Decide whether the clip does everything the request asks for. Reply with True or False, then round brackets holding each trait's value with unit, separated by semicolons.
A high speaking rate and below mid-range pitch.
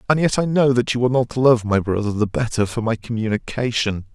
True (230 wpm; 120 Hz)